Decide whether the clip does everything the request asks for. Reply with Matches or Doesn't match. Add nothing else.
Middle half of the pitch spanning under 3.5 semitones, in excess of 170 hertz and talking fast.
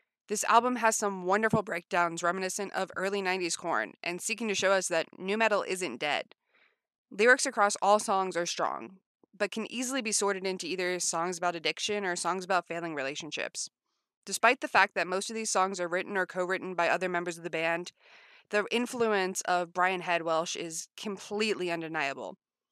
Doesn't match